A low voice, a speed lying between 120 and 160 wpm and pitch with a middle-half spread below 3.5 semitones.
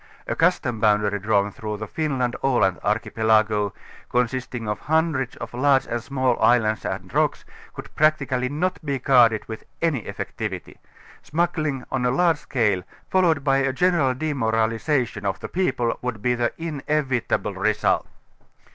No: low, 125 Hz; average, 155 wpm; average, 4.6 semitones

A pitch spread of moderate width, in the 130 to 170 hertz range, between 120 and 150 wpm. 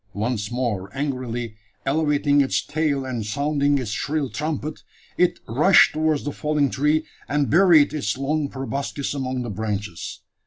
Yes: average, 3.7 semitones; medium, 140 Hz; average, 145 wpm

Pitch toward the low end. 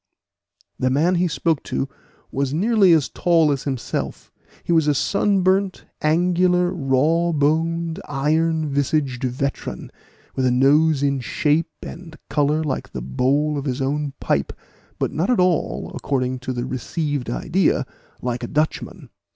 No: medium, 150 Hz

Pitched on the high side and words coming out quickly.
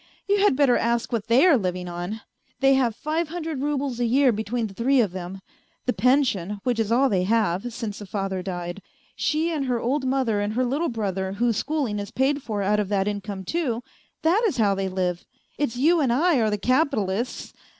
Yes: high, 235 Hz; fast, 210 wpm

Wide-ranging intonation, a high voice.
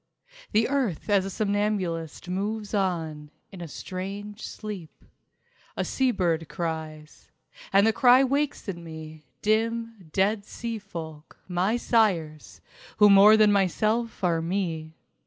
No: average, 4.6 semitones; high, 195 Hz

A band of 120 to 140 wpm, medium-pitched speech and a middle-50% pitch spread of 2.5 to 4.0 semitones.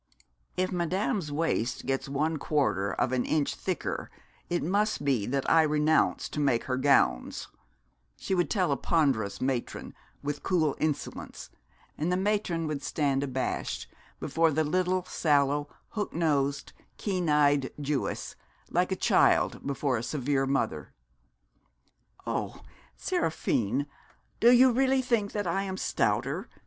No: slow, 135 wpm; medium, 150 Hz; average, 4.8 semitones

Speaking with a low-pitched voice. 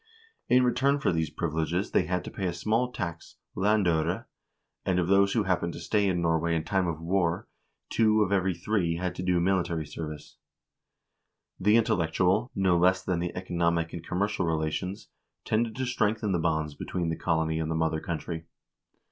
Yes: very low, 90 Hz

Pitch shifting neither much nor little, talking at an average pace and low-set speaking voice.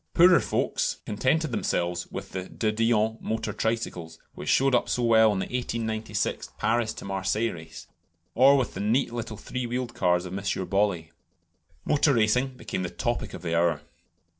Yes: average, 4.3 semitones; average, 165 wpm; low, 110 Hz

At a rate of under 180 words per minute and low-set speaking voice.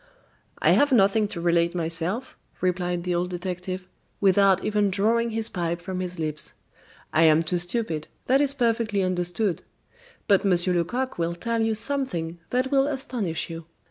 No: average, 160 wpm; medium, 185 Hz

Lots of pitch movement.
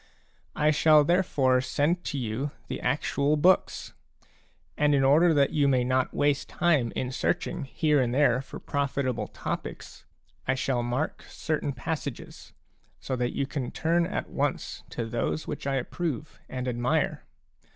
No: average, 3.0 semitones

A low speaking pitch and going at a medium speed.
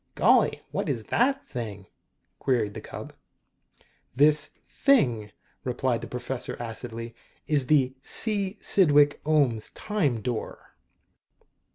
No: low, 130 Hz; slow, 105 wpm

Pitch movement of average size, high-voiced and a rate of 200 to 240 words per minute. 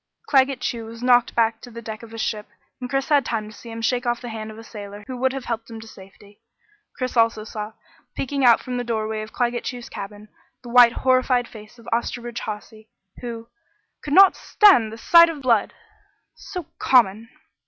No: narrow, 2.3 semitones; high, 235 Hz; fast, 205 wpm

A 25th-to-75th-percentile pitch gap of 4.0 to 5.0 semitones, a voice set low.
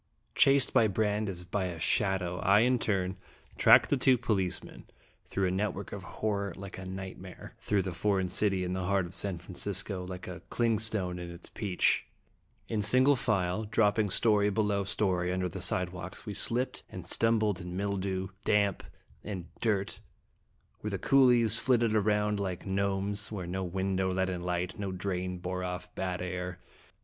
No: narrow, 2.4 semitones; very low, 95 Hz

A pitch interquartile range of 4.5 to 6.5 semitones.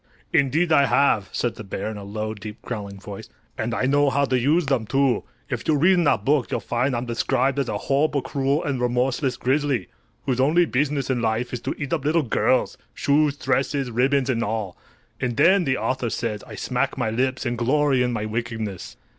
No: average, 3.6 semitones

